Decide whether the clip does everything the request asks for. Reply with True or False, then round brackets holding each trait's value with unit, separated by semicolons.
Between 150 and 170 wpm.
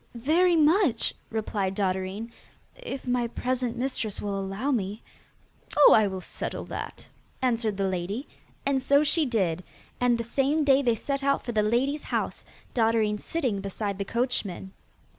True (155 wpm)